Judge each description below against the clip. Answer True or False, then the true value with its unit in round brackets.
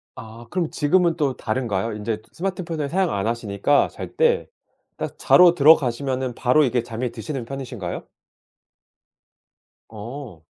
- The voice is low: True (130 Hz)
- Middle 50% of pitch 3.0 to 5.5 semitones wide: True (5.2 semitones)